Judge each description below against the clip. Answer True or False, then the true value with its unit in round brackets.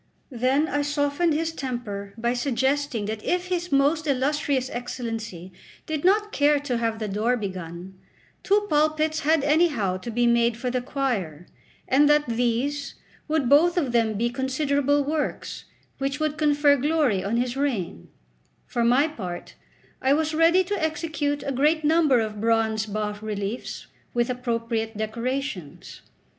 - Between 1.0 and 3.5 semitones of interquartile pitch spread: False (4.7 semitones)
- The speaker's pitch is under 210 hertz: False (265 Hz)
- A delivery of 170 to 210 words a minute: False (150 wpm)